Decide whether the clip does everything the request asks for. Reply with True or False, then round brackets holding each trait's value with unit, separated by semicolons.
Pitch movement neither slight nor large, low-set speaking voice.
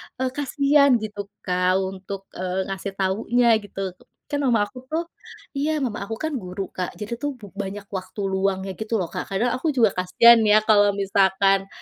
False (4.1 semitones; 205 Hz)